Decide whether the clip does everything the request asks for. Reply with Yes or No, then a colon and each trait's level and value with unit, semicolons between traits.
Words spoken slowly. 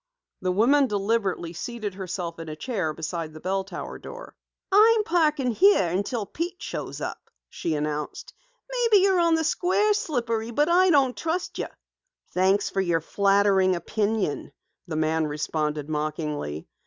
No: average, 150 wpm